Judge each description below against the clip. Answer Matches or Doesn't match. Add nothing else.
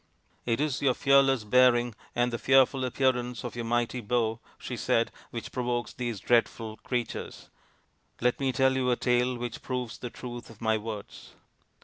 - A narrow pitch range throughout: Matches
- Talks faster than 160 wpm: Matches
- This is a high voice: Doesn't match